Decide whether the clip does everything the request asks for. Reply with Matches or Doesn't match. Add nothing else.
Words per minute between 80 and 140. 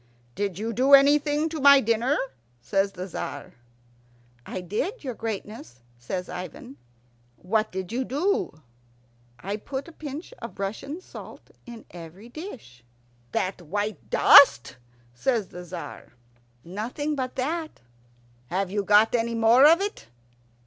Matches